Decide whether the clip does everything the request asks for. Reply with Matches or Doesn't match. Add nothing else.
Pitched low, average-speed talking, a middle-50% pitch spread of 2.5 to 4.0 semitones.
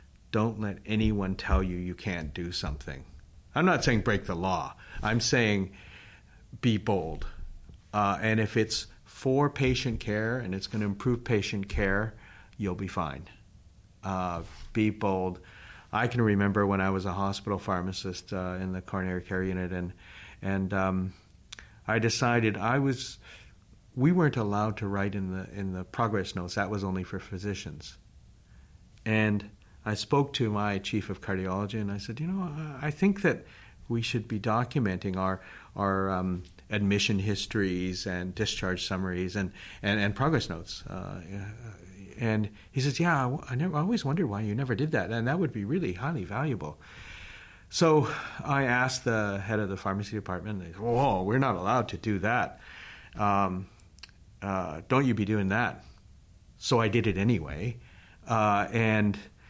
Matches